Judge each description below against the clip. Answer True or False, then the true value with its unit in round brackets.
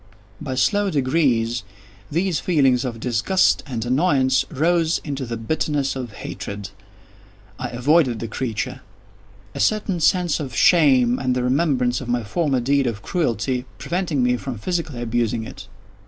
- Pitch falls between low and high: False (130 Hz)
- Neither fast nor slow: True (145 wpm)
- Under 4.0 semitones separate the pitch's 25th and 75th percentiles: False (4.8 semitones)